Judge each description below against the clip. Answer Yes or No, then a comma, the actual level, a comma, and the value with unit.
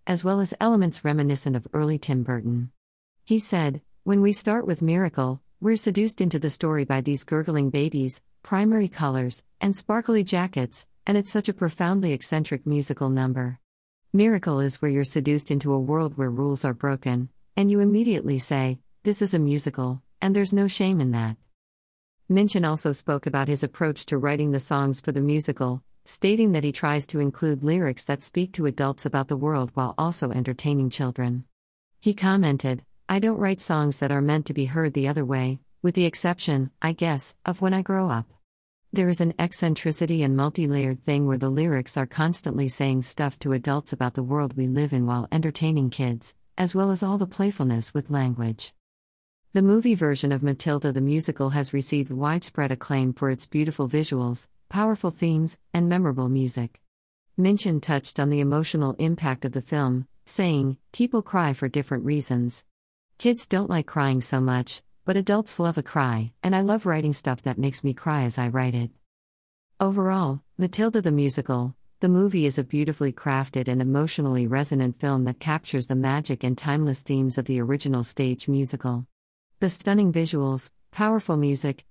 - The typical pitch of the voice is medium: Yes, medium, 145 Hz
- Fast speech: No, average, 180 wpm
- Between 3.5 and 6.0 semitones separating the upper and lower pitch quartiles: Yes, average, 4.7 semitones